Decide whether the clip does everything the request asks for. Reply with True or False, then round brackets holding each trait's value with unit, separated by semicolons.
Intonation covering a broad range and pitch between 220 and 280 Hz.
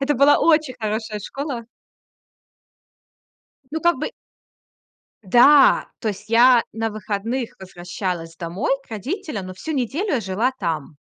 True (6.5 semitones; 230 Hz)